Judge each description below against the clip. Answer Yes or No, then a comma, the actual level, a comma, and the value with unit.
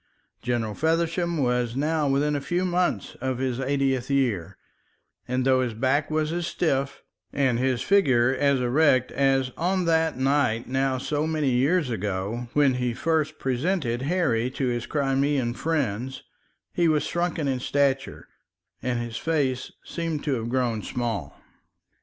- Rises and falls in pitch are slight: No, average, 3.9 semitones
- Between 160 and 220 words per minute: No, average, 150 wpm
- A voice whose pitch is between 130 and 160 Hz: Yes, low, 135 Hz